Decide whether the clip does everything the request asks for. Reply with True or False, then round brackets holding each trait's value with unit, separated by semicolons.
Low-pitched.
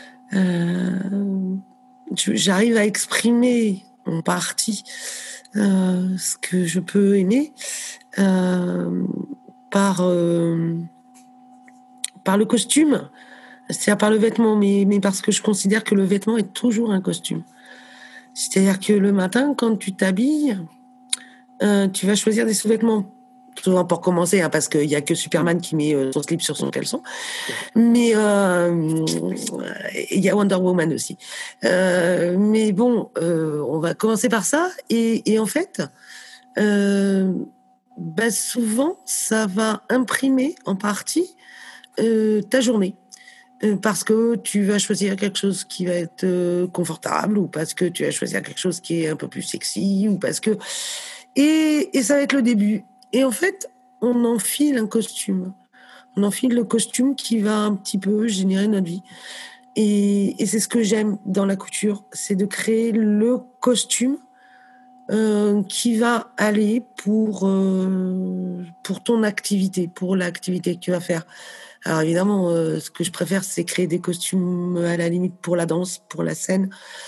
False (205 Hz)